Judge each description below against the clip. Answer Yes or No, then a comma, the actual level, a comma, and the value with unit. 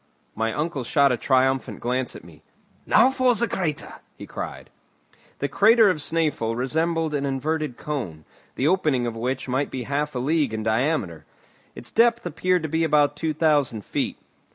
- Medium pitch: Yes, medium, 145 Hz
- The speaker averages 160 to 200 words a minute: Yes, average, 175 wpm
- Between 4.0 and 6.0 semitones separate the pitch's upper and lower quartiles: Yes, average, 4.3 semitones